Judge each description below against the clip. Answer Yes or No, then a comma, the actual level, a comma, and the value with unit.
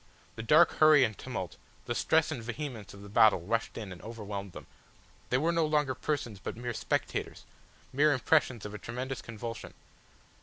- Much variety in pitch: Yes, wide, 5.7 semitones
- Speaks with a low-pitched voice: Yes, low, 120 Hz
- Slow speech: No, average, 180 wpm